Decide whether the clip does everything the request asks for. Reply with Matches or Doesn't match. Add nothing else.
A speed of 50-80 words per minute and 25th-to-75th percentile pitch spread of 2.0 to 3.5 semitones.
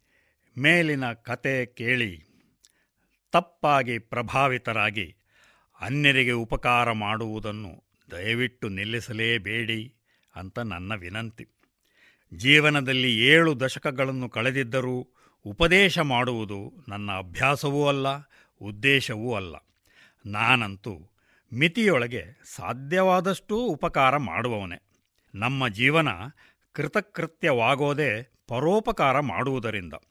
Doesn't match